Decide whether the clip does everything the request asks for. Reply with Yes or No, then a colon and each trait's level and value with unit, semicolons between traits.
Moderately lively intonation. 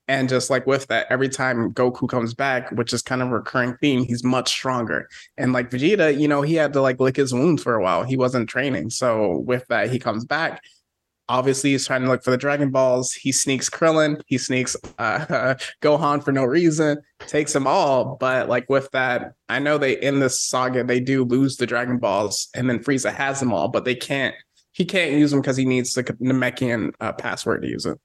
No: narrow, 1.7 semitones